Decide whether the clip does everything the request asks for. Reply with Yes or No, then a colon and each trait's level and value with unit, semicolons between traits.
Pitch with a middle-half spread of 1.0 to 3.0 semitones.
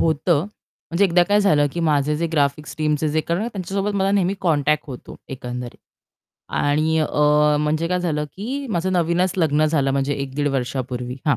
No: average, 3.6 semitones